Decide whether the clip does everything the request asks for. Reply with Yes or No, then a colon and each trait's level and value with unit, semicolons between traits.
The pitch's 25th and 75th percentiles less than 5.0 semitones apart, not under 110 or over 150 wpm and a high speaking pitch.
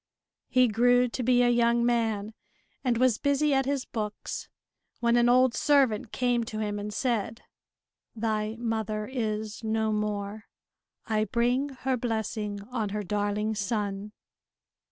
Yes: narrow, 2.6 semitones; average, 140 wpm; high, 225 Hz